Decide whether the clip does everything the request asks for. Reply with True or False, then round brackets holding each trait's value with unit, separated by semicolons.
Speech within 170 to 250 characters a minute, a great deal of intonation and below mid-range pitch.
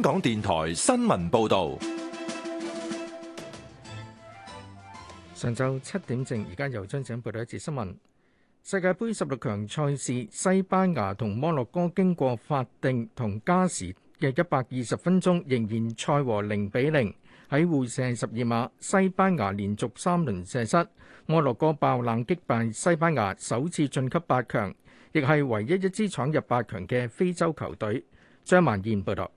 True (225 characters per minute; 7.9 semitones; 130 Hz)